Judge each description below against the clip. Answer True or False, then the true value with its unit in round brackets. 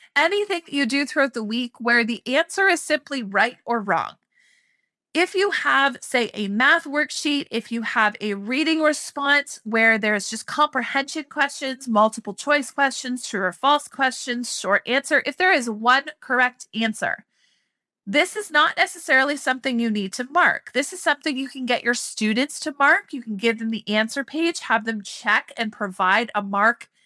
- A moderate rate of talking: True (180 wpm)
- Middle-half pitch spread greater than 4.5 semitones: True (4.9 semitones)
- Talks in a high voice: True (265 Hz)